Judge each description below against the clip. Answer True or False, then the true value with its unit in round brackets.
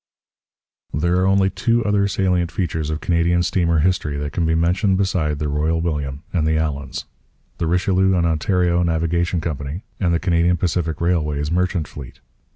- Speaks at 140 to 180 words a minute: True (165 wpm)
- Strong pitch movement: False (2.7 semitones)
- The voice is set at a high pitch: False (85 Hz)